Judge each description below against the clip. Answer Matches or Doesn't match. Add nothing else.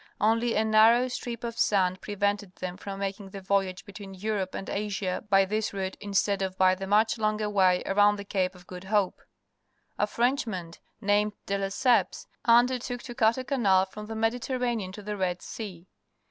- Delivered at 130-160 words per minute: Doesn't match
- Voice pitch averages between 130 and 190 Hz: Doesn't match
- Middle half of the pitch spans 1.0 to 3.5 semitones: Matches